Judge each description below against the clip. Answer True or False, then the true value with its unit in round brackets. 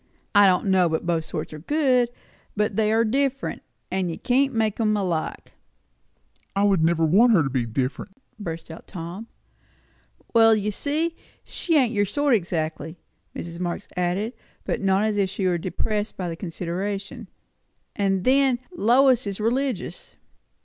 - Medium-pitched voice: False (205 Hz)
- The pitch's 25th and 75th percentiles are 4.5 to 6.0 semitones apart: True (5.1 semitones)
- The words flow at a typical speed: True (160 wpm)